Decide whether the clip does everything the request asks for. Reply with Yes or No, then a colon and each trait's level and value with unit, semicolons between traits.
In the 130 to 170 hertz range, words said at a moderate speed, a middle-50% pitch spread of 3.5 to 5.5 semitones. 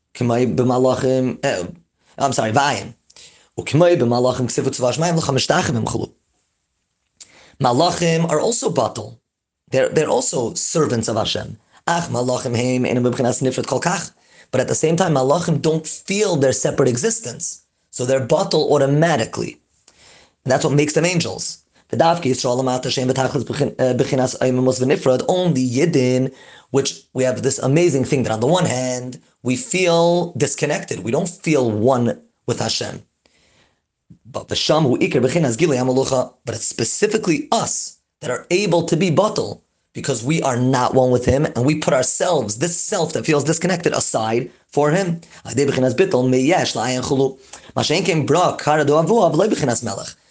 No: low, 135 Hz; slow, 130 wpm; average, 4.4 semitones